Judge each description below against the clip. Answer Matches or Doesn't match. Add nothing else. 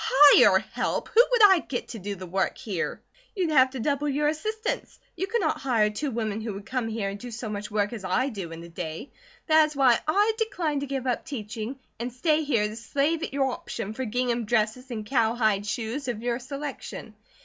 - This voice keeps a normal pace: Doesn't match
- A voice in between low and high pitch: Doesn't match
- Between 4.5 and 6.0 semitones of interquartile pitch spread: Matches